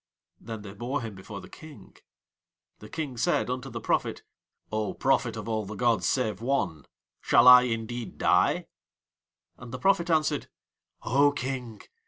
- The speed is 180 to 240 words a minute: No, average, 155 wpm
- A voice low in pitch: Yes, low, 120 Hz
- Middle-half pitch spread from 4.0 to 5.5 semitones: No, average, 3.5 semitones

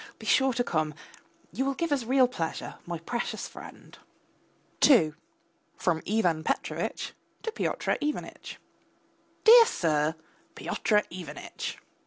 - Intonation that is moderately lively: No, wide, 8.8 semitones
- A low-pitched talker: No, high, 215 Hz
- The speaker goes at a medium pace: No, slow, 120 wpm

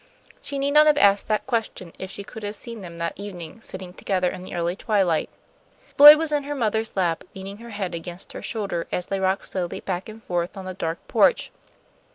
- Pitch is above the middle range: Yes, high, 195 Hz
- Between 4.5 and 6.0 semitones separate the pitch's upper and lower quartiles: No, average, 3.9 semitones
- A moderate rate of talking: No, fast, 215 wpm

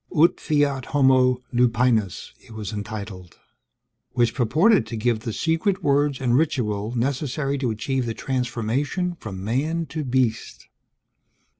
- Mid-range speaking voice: No, low, 125 Hz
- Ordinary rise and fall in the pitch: Yes, average, 4.5 semitones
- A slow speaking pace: Yes, slow, 130 wpm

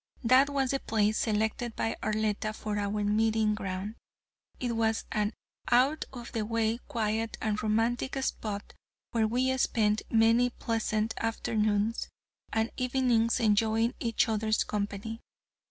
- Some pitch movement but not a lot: No, narrow, 1.6 semitones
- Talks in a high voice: Yes, high, 225 Hz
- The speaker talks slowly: Yes, slow, 130 wpm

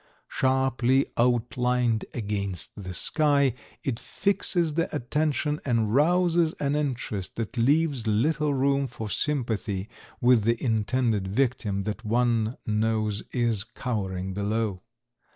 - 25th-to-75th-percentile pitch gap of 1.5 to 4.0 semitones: No, average, 4.6 semitones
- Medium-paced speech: No, slow, 115 wpm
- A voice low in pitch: Yes, low, 120 Hz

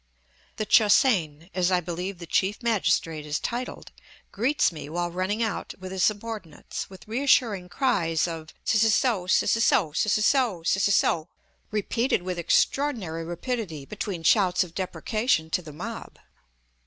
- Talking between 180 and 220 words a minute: No, average, 165 wpm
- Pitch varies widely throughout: No, average, 4.8 semitones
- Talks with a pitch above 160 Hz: Yes, medium, 185 Hz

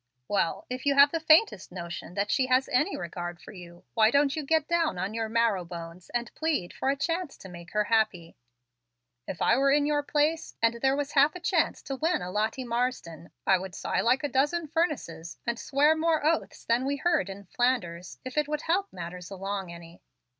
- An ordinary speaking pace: No, fast, 210 wpm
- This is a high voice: Yes, high, 245 Hz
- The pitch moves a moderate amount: No, wide, 8.2 semitones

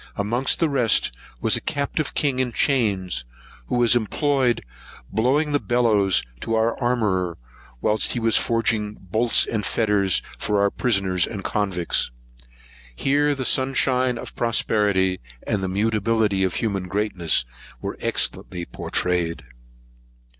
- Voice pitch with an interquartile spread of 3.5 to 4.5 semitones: Yes, average, 4.2 semitones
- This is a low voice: Yes, low, 110 Hz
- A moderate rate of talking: No, slow, 130 wpm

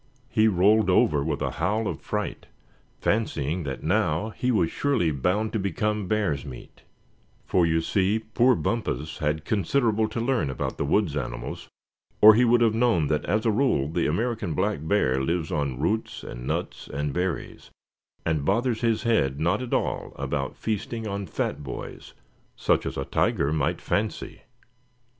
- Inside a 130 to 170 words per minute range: Yes, average, 165 wpm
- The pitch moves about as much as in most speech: No, wide, 6.5 semitones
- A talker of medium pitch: No, very low, 95 Hz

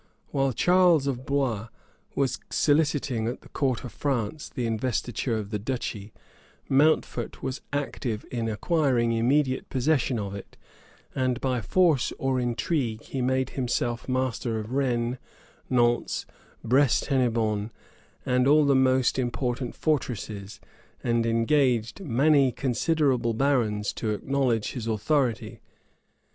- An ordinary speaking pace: No, slow, 125 wpm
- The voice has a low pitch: Yes, low, 125 Hz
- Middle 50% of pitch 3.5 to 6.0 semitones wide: No, average, 3.1 semitones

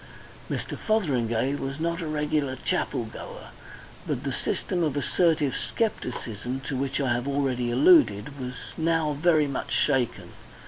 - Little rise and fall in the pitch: No, average, 3.7 semitones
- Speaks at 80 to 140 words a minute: Yes, slow, 135 wpm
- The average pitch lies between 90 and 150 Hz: Yes, medium, 140 Hz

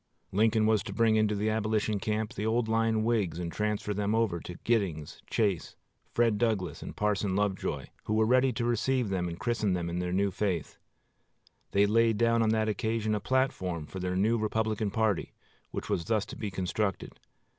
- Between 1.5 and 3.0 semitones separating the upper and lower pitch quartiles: Yes, narrow, 2.5 semitones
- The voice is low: Yes, low, 105 Hz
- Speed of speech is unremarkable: Yes, average, 190 wpm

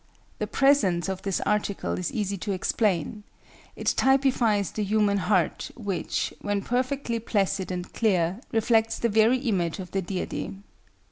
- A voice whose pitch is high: Yes, high, 205 Hz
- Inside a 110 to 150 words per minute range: Yes, average, 145 wpm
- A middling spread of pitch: Yes, average, 3.3 semitones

